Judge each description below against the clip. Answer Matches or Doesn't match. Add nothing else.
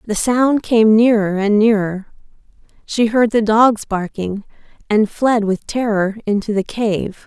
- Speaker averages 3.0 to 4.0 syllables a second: Matches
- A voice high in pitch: Matches